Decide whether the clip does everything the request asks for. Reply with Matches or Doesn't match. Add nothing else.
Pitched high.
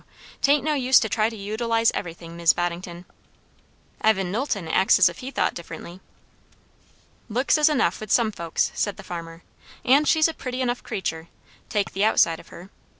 Matches